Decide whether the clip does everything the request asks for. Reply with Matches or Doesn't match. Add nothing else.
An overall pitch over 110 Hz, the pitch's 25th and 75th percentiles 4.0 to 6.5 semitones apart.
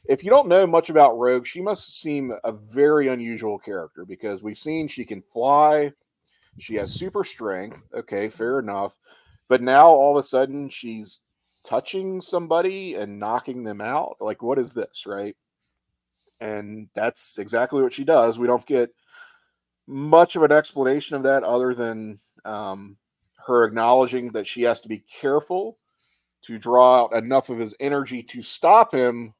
Matches